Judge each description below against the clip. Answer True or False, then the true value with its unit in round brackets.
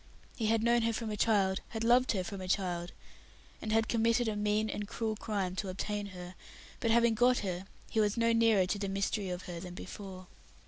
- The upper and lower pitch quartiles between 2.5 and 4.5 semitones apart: True (3.1 semitones)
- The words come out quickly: True (220 wpm)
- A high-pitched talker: True (210 Hz)